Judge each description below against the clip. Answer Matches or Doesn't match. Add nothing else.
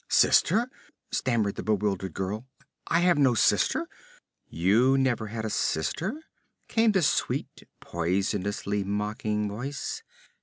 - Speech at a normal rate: Doesn't match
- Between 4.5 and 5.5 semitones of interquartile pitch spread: Matches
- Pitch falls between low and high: Doesn't match